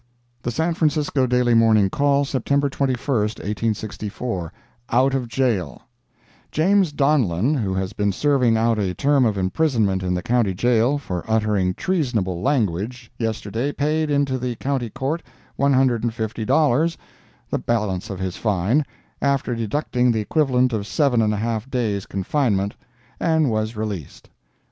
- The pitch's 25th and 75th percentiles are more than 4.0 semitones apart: Yes, average, 4.9 semitones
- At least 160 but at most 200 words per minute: No, average, 150 wpm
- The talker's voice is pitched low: Yes, low, 120 Hz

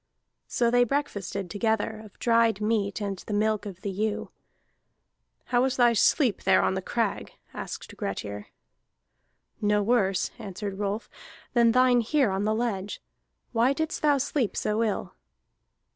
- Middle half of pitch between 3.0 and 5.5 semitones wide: Yes, average, 3.3 semitones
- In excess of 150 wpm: No, average, 145 wpm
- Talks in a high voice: Yes, high, 215 Hz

